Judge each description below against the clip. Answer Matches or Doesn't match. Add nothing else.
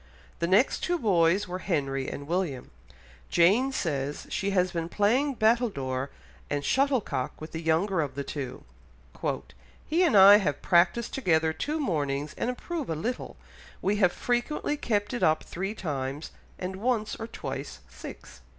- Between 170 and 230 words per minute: Doesn't match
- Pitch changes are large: Matches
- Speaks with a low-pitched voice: Doesn't match